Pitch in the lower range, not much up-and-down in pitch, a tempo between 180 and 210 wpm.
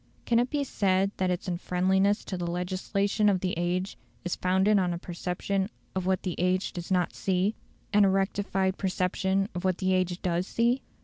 No: medium, 185 Hz; narrow, 1.6 semitones; average, 190 wpm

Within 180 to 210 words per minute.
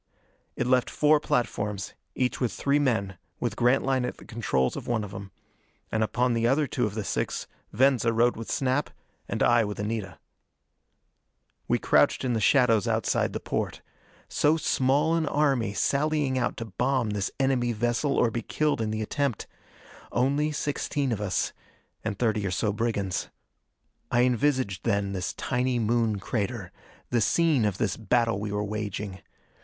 No: average, 165 wpm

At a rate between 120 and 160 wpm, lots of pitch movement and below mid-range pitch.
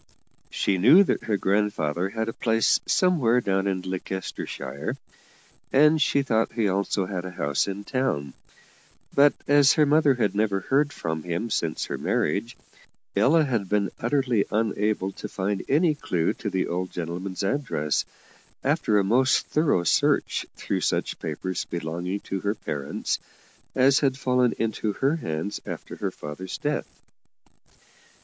Yes: average, 150 wpm; wide, 6.0 semitones; low, 105 Hz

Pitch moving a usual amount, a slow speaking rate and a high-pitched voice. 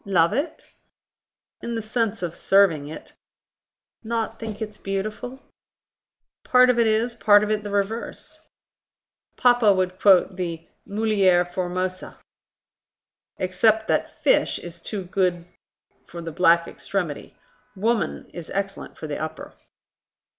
Yes: average, 3.7 semitones; slow, 125 wpm; high, 200 Hz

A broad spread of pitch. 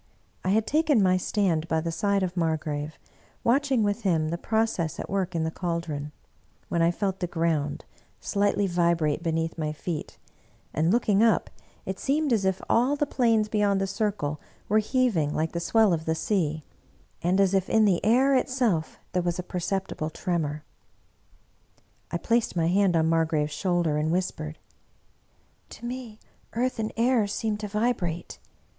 No: average, 4.9 semitones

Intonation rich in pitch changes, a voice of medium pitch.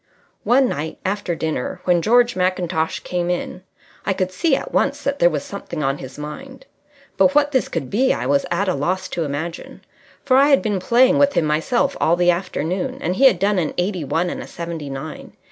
Yes: wide, 7.3 semitones; medium, 180 Hz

